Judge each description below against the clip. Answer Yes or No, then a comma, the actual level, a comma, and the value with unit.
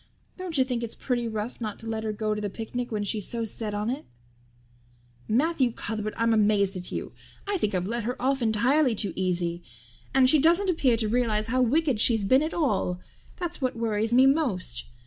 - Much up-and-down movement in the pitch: No, average, 3.7 semitones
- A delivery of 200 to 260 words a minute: Yes, fast, 205 wpm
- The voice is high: Yes, high, 230 Hz